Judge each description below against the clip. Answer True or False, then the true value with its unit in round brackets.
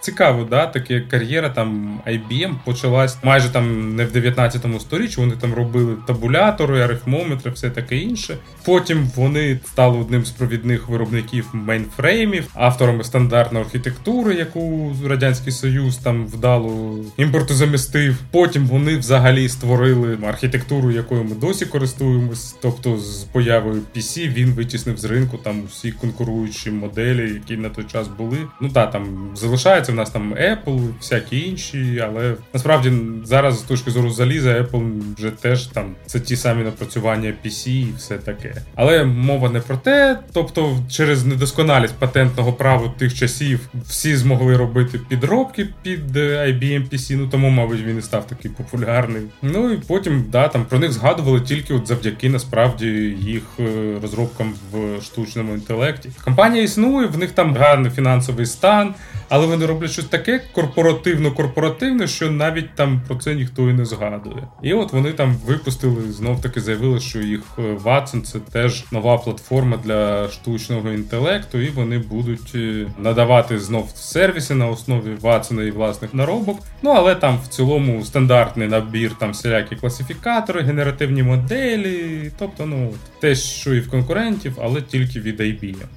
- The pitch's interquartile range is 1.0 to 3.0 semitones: False (3.5 semitones)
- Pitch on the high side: False (125 Hz)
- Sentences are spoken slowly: False (150 wpm)